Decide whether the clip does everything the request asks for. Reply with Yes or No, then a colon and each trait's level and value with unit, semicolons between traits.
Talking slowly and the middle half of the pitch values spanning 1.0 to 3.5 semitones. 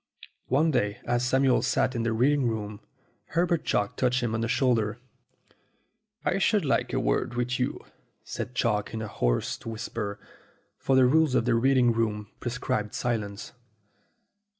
No: average, 165 wpm; average, 2.9 semitones